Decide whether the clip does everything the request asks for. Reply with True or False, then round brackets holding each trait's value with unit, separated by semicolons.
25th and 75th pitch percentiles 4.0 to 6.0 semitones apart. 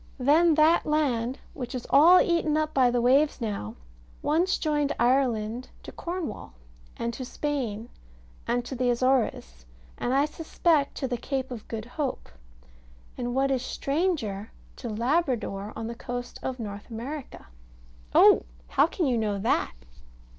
True (4.3 semitones)